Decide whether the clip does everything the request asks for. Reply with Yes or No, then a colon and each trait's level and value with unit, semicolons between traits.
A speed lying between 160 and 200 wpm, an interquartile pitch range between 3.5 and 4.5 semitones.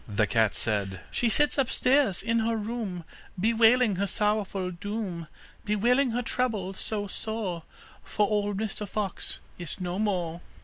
No: average, 140 wpm; average, 4.0 semitones